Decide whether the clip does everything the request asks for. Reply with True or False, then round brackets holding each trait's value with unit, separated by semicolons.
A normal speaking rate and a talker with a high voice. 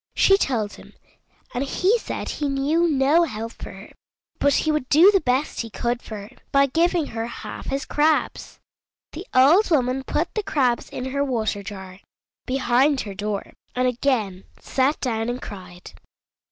True (170 wpm; 260 Hz)